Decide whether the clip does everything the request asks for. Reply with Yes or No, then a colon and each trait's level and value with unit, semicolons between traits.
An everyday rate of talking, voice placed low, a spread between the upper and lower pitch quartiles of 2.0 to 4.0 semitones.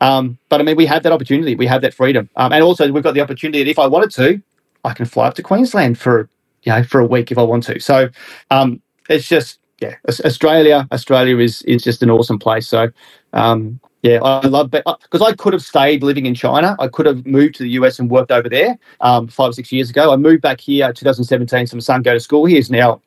No: fast, 255 wpm; low, 130 Hz; average, 3.4 semitones